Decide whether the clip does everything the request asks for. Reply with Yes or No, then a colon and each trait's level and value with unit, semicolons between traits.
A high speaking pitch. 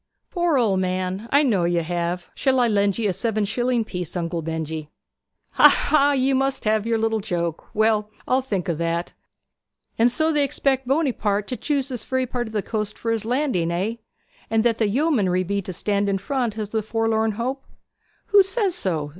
Yes: high, 220 Hz